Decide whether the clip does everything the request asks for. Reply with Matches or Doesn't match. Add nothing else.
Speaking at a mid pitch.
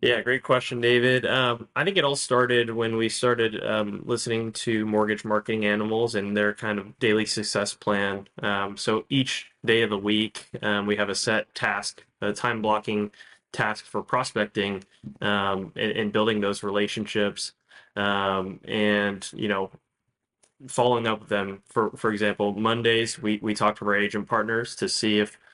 Doesn't match